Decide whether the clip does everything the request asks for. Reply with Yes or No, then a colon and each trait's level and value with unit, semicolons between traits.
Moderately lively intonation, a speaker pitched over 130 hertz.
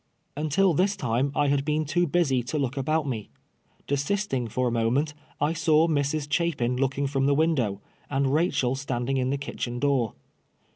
Yes: average, 3.3 semitones; medium, 140 Hz